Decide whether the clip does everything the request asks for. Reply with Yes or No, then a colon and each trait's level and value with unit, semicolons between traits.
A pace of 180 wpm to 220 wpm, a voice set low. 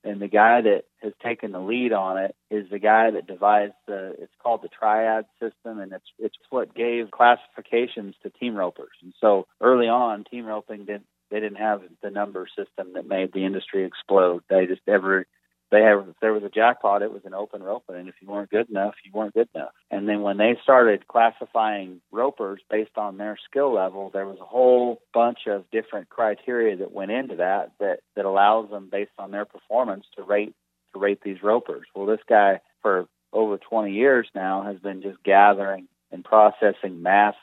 Yes: average, 200 wpm; low, 105 Hz